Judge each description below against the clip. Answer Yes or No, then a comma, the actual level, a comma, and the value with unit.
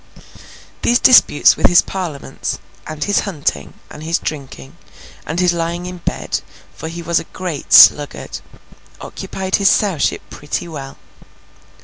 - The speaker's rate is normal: No, slow, 125 wpm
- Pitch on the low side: No, medium, 170 Hz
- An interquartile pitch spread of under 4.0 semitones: Yes, average, 3.4 semitones